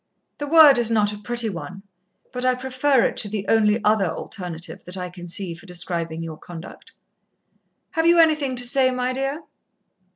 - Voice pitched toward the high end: Yes, high, 220 Hz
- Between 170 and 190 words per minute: Yes, average, 185 wpm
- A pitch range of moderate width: No, wide, 6.4 semitones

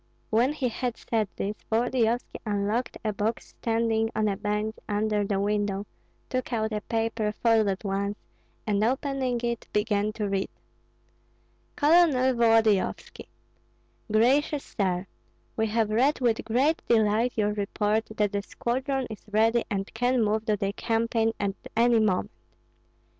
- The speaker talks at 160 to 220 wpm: No, average, 140 wpm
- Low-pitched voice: No, high, 220 Hz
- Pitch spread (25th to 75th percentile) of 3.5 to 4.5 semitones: No, narrow, 2.4 semitones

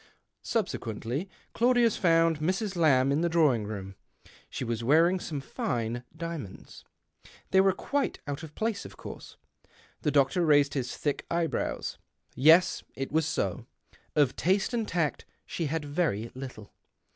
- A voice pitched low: No, medium, 155 Hz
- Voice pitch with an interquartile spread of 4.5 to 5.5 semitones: Yes, average, 5.1 semitones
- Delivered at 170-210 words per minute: No, average, 150 wpm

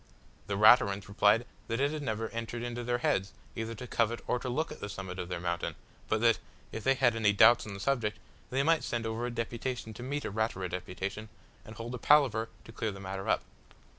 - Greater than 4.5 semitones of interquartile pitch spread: No, average, 2.9 semitones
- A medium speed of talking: No, fast, 225 wpm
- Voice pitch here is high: No, low, 115 Hz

